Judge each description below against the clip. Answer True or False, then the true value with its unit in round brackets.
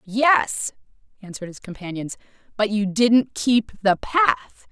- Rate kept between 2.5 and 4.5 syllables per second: True (3.8 syllables/s)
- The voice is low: False (215 Hz)